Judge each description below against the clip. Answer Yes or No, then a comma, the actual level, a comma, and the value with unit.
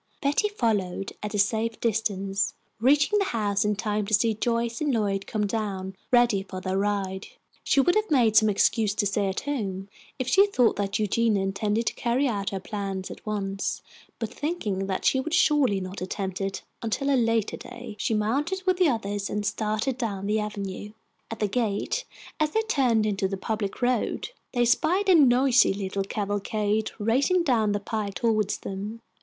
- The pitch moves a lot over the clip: No, average, 3.6 semitones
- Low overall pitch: No, high, 215 Hz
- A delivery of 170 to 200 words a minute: Yes, average, 185 wpm